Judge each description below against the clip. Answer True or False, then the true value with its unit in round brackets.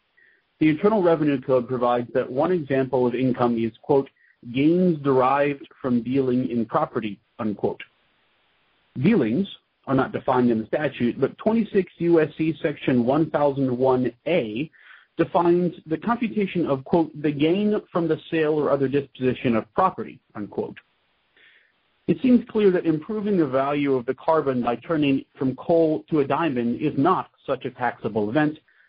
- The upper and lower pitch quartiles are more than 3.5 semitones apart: True (4.5 semitones)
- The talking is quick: False (145 wpm)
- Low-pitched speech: False (145 Hz)